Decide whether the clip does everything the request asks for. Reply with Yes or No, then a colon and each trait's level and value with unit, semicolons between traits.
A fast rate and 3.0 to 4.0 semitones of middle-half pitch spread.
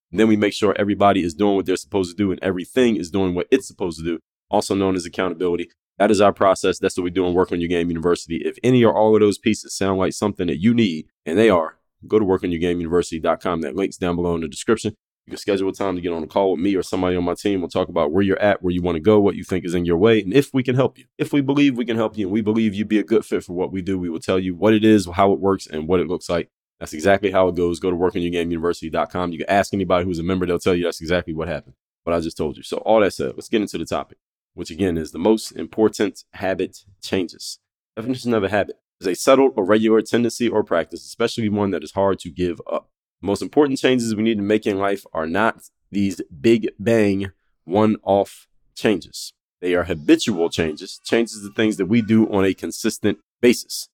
Yes: fast, 265 wpm; average, 3.5 semitones